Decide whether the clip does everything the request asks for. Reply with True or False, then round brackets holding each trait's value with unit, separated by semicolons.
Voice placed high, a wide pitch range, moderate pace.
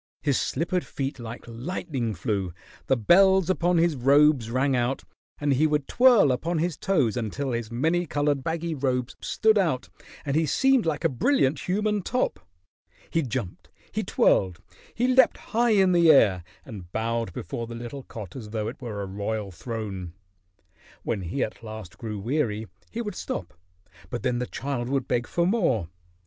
False (135 Hz; 6.8 semitones; 175 wpm)